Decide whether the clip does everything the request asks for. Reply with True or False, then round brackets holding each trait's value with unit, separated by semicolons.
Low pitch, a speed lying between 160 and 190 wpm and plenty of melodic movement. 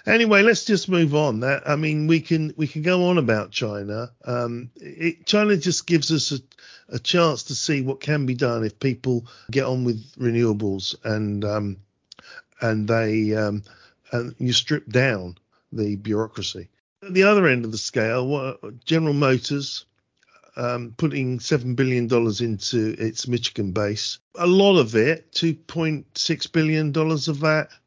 True (130 Hz; 165 wpm; 5.9 semitones)